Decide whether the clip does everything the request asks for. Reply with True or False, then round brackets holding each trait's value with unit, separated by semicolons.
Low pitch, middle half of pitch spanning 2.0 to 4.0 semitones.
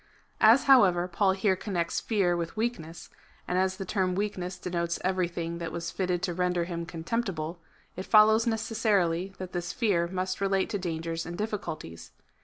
False (185 Hz; 2.9 semitones)